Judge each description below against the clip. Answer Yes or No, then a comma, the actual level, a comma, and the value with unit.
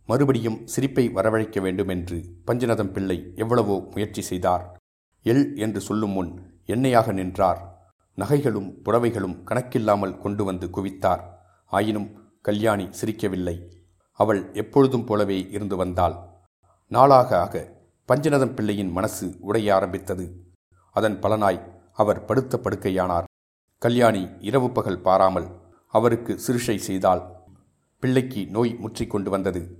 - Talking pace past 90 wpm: Yes, average, 110 wpm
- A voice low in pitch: Yes, low, 100 Hz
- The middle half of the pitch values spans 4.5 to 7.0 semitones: No, average, 3.6 semitones